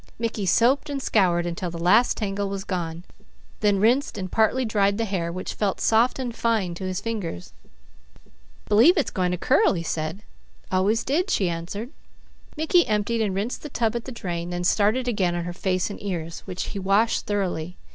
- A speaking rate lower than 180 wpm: No, average, 190 wpm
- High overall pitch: Yes, high, 200 Hz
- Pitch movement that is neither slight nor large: Yes, average, 4.2 semitones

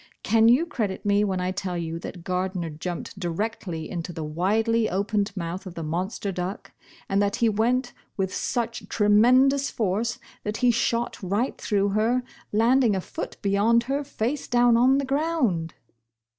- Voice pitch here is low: No, high, 210 Hz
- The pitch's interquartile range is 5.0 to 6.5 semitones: No, average, 4.4 semitones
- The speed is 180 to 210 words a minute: No, average, 170 wpm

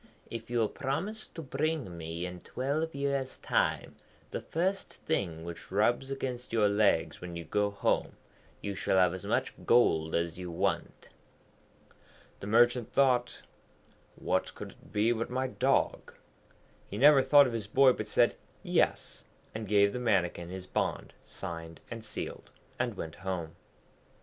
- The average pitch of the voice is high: No, low, 110 Hz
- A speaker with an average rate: Yes, average, 155 wpm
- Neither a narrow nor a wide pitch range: No, wide, 6.4 semitones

